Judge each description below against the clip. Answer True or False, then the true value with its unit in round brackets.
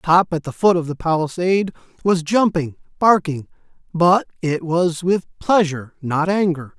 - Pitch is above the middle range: False (170 Hz)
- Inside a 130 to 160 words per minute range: True (150 wpm)